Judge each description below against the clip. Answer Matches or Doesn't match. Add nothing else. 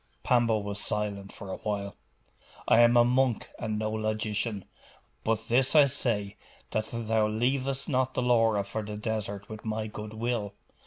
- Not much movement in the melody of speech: Matches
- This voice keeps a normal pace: Matches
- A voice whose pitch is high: Doesn't match